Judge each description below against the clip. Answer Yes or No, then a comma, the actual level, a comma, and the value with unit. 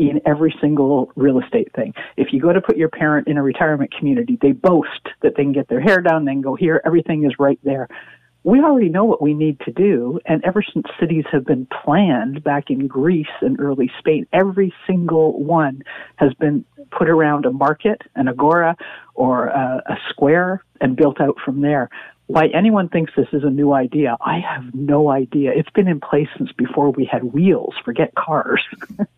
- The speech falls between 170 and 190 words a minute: No, average, 200 wpm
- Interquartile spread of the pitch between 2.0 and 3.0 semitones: No, average, 3.6 semitones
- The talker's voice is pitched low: No, medium, 150 Hz